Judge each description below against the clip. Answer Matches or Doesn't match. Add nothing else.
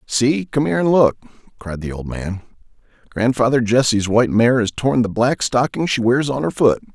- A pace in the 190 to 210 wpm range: Matches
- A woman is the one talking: Doesn't match